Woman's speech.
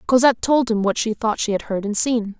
Yes: female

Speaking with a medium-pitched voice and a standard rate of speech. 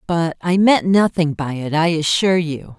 Yes: medium, 165 Hz; average, 195 wpm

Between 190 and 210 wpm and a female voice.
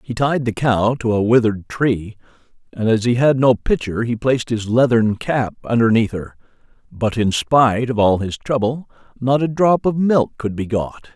No: average, 195 wpm; male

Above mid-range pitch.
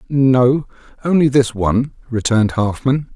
No: low, 125 Hz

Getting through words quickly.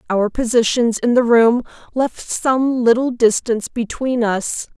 No: average, 140 wpm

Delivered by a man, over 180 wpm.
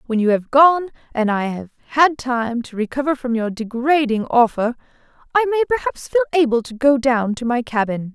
No: female; average, 190 wpm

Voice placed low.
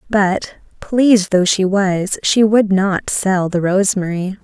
No: high, 195 Hz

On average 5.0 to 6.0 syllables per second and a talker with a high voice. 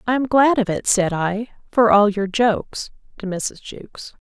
No: 4.5 syllables/s; high, 215 Hz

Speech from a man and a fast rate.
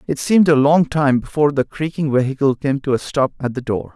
Yes: male; fast, 240 wpm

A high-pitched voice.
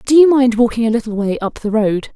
Yes: high, 230 Hz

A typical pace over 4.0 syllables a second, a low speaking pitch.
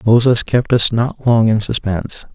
Yes: 4.6 syllables/s; low, 115 Hz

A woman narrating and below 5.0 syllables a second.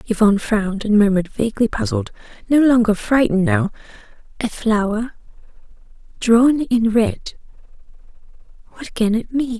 No: female; 5.1 syllables/s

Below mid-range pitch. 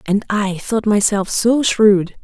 No: high, 210 Hz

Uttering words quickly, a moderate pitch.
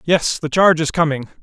Yes: fast, 210 wpm; medium, 160 Hz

